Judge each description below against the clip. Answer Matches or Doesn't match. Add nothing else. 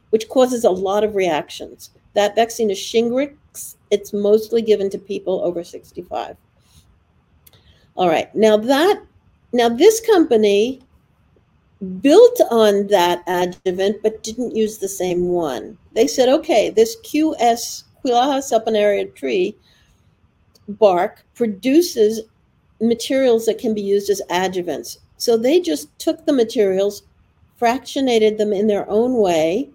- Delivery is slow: Matches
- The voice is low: Doesn't match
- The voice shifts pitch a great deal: Doesn't match